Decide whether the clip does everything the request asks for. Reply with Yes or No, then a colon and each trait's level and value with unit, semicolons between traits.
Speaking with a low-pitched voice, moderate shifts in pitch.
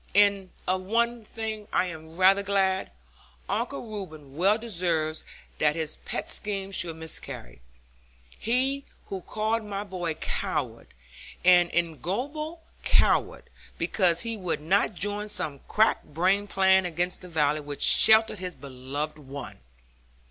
No: medium, 185 Hz; average, 4.6 semitones